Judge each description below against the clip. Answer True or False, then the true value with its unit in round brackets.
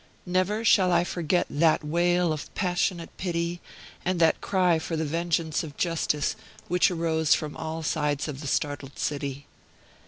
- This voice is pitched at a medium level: True (165 Hz)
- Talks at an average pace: True (155 wpm)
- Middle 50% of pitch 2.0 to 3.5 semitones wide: True (2.7 semitones)